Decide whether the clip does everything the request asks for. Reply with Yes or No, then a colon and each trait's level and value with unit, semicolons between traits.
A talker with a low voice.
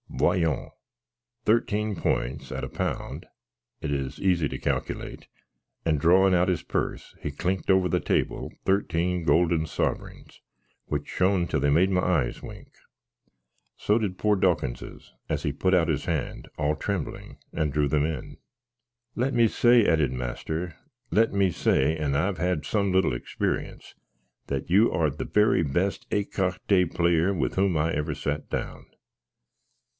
Yes: very low, 85 Hz